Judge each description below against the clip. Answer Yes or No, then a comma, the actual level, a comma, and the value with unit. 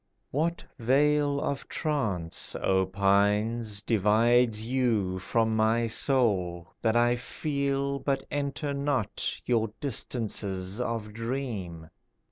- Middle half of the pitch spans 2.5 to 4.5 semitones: No, average, 5.1 semitones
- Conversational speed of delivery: No, slow, 100 wpm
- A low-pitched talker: Yes, low, 115 Hz